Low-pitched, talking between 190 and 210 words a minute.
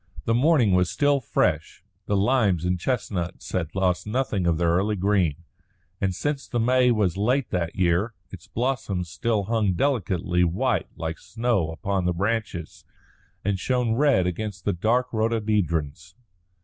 No: low, 100 Hz; average, 150 wpm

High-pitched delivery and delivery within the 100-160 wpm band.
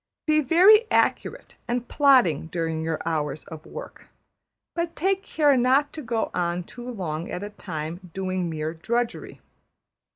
Yes: high, 195 Hz; average, 150 wpm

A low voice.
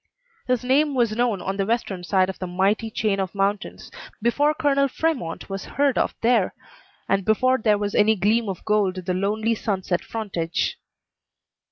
No: high, 210 Hz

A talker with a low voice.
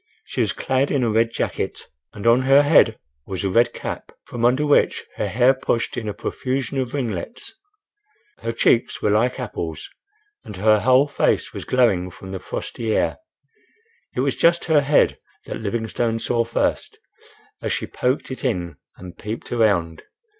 Yes: low, 115 Hz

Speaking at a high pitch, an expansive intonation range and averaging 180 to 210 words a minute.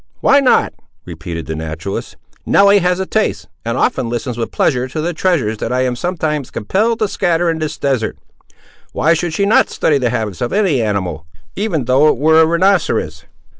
No: medium, 150 Hz; wide, 7.8 semitones; average, 190 wpm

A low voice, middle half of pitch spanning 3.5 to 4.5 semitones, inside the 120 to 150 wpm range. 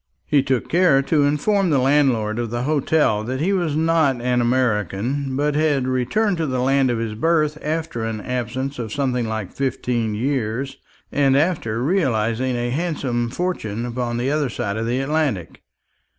No: low, 130 Hz; average, 4.0 semitones; average, 170 wpm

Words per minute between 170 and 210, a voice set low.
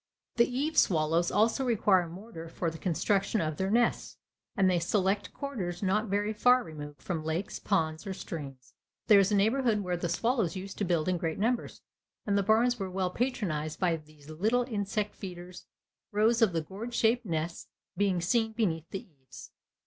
No: average, 180 wpm; high, 190 Hz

